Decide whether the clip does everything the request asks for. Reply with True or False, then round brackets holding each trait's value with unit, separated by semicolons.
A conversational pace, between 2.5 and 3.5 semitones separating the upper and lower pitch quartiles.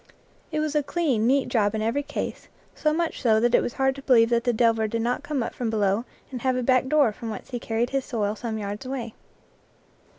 False (240 wpm; 3.2 semitones)